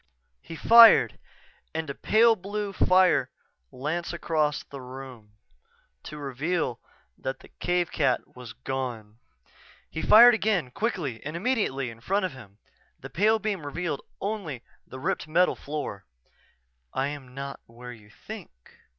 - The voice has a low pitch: No, medium, 150 Hz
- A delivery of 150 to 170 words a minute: No, slow, 135 wpm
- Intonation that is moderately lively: No, wide, 6.6 semitones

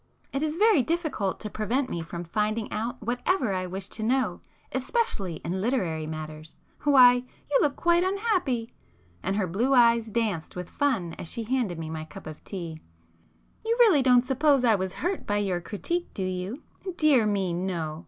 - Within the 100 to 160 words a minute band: No, average, 175 wpm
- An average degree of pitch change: No, wide, 7.2 semitones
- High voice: Yes, high, 220 Hz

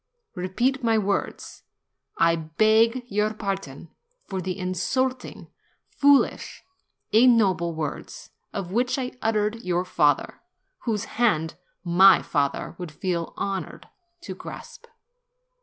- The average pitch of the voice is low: No, high, 195 Hz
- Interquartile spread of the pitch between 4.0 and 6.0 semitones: Yes, average, 4.8 semitones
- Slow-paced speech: Yes, slow, 115 wpm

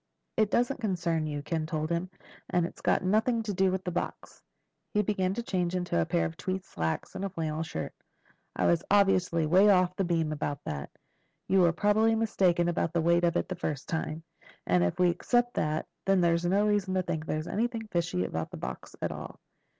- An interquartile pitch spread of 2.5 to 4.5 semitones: Yes, average, 3.5 semitones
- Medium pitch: Yes, medium, 175 Hz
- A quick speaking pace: Yes, fast, 210 wpm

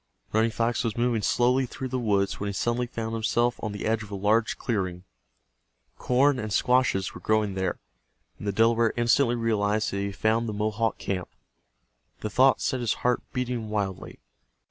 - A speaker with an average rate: Yes, average, 185 wpm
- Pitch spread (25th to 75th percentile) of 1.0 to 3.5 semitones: Yes, average, 2.8 semitones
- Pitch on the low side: Yes, low, 110 Hz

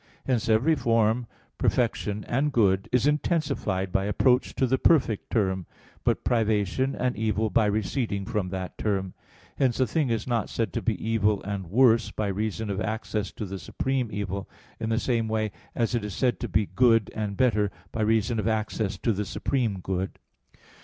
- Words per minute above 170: Yes, average, 180 wpm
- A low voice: Yes, low, 110 Hz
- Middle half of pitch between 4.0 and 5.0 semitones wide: No, average, 3.2 semitones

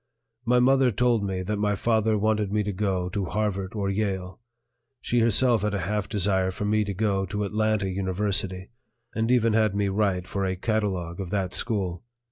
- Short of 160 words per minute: No, average, 190 wpm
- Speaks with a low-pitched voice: Yes, low, 105 Hz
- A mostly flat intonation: Yes, narrow, 2.3 semitones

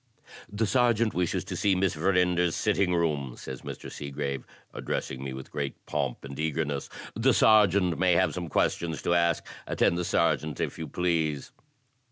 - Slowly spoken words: No, average, 165 wpm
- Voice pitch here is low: Yes, very low, 85 Hz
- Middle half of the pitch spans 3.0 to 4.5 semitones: Yes, average, 4.2 semitones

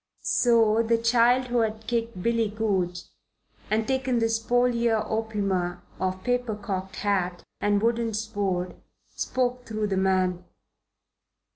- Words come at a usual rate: No, slow, 125 wpm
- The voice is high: Yes, high, 220 Hz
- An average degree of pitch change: Yes, average, 3.4 semitones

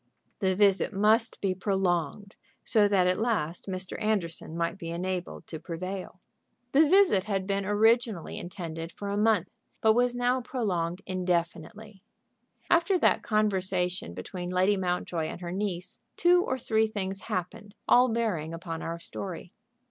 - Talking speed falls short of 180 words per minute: Yes, average, 150 wpm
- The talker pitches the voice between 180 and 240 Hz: Yes, high, 190 Hz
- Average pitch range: Yes, average, 3.6 semitones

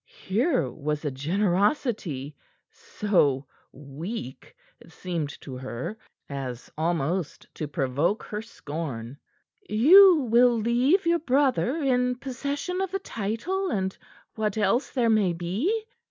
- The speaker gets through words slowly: Yes, slow, 120 wpm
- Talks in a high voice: Yes, high, 210 Hz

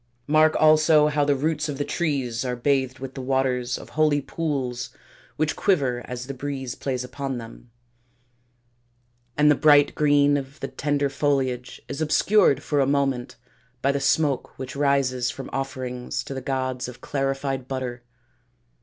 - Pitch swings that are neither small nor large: No, narrow, 2.1 semitones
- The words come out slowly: No, average, 160 wpm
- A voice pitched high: No, low, 135 Hz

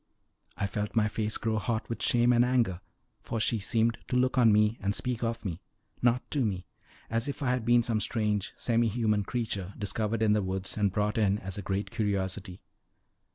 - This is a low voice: Yes, low, 110 Hz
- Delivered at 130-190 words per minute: No, average, 200 wpm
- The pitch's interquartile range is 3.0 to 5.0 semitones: No, narrow, 2.6 semitones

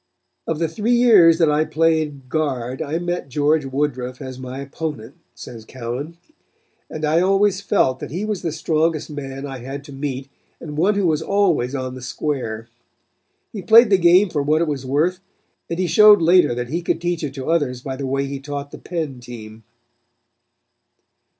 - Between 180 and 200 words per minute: Yes, average, 190 wpm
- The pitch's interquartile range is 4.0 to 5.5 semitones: Yes, average, 4.3 semitones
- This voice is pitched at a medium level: Yes, medium, 150 Hz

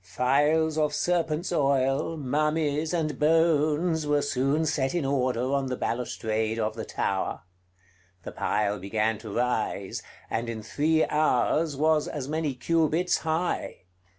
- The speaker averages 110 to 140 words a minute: Yes, slow, 135 wpm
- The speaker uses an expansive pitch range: No, average, 4.2 semitones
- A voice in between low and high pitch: Yes, medium, 145 Hz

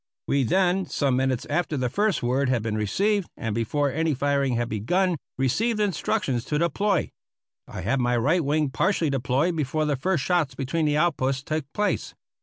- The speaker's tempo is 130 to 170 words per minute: No, average, 180 wpm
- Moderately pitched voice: Yes, medium, 145 Hz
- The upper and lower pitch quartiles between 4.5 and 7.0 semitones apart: Yes, average, 5.2 semitones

